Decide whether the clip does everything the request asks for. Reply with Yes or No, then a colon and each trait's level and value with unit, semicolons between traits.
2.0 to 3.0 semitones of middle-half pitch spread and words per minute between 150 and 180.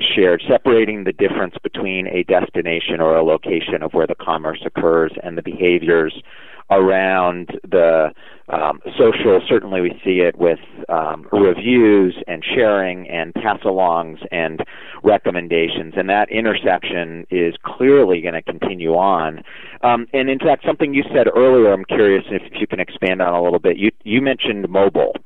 No: average, 3.8 semitones; average, 165 wpm